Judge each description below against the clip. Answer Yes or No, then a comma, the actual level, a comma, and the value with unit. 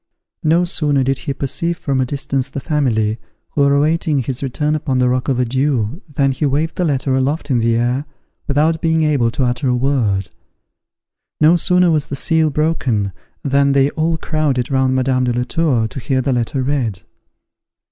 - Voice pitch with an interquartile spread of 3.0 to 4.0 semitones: Yes, average, 3.3 semitones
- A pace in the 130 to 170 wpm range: No, average, 190 wpm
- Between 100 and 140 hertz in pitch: Yes, low, 135 Hz